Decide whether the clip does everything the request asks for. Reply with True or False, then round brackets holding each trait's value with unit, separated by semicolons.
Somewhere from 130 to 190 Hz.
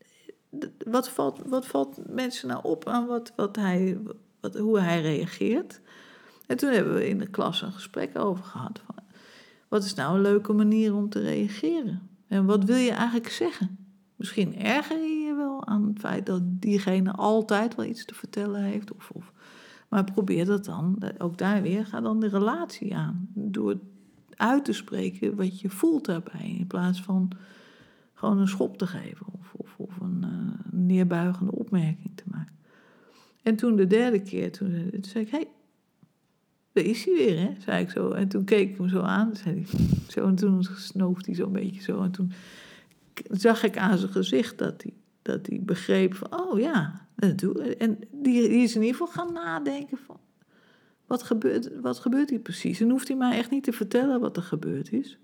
False (205 Hz)